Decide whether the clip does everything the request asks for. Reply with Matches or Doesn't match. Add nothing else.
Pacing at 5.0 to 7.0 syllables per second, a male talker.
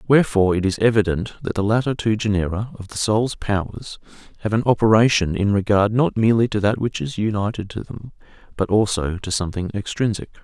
Matches